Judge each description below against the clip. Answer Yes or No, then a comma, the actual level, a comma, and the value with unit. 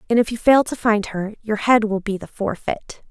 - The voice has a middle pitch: No, high, 215 Hz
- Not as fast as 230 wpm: No, fast, 250 wpm